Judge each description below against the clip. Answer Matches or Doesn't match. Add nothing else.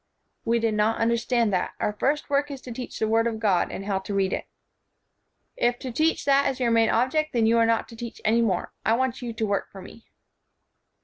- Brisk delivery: Matches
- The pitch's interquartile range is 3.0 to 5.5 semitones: Doesn't match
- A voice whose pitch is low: Doesn't match